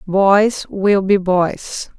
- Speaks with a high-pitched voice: Yes, high, 195 Hz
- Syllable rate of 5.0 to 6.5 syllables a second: No, 2.3 syllables/s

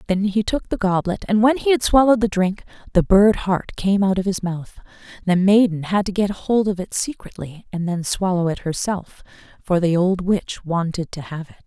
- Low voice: No, high, 190 Hz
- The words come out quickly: Yes, fast, 215 wpm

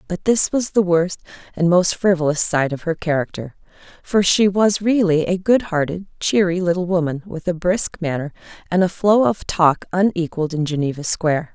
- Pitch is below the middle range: No, medium, 175 Hz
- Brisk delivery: No, average, 180 wpm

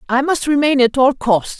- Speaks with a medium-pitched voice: No, very high, 265 Hz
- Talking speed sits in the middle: No, fast, 225 wpm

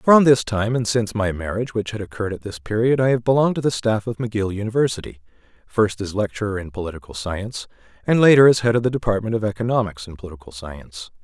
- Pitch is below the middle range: Yes, low, 105 Hz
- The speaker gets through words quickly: Yes, fast, 215 wpm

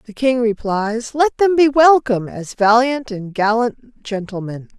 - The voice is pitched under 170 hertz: No, high, 235 Hz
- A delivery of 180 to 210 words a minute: No, average, 150 wpm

